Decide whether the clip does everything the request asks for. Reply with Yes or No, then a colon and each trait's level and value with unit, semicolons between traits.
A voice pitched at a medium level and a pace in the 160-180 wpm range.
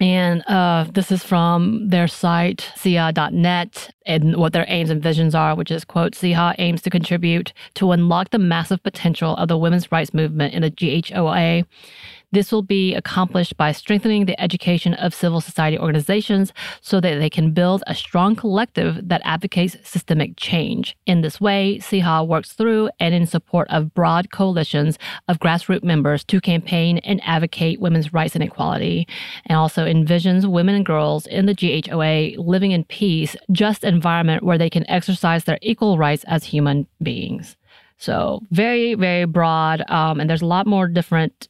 Yes: medium, 175 Hz; average, 170 wpm